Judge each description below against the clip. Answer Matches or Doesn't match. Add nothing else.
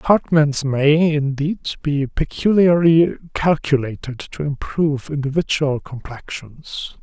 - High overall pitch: Doesn't match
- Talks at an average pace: Doesn't match